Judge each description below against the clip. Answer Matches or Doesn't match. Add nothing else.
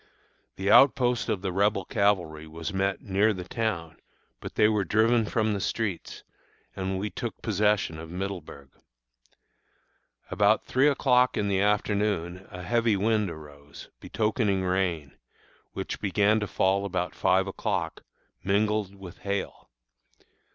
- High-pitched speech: Doesn't match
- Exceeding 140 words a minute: Doesn't match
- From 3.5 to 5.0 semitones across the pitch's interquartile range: Doesn't match